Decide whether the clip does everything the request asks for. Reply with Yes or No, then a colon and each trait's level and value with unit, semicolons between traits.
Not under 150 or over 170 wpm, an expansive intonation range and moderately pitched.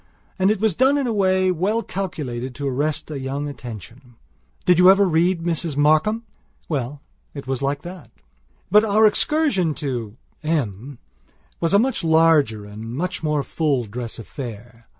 Yes: average, 160 wpm; wide, 6.6 semitones; medium, 155 Hz